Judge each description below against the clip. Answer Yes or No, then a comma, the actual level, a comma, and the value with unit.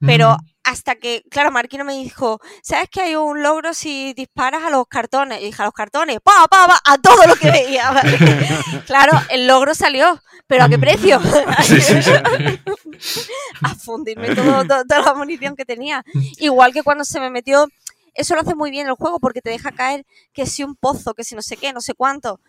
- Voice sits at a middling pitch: No, very high, 270 Hz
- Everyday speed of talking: No, fast, 205 wpm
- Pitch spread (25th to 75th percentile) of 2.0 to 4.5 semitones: Yes, average, 3.4 semitones